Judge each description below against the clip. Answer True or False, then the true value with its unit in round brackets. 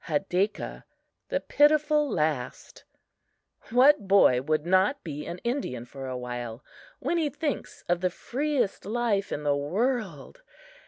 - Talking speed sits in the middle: False (130 wpm)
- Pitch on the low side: False (195 Hz)